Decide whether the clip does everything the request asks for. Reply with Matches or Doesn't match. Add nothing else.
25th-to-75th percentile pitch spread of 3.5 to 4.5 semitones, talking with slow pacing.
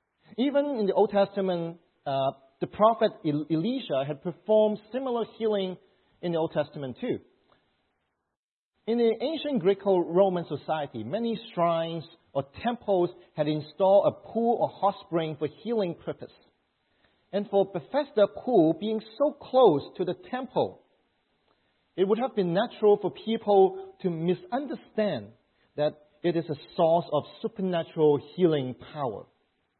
Doesn't match